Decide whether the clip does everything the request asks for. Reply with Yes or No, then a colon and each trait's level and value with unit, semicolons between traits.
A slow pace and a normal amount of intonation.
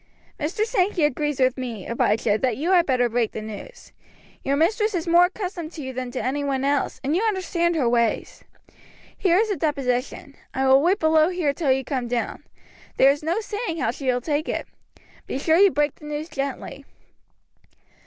No: average, 195 wpm; average, 5.0 semitones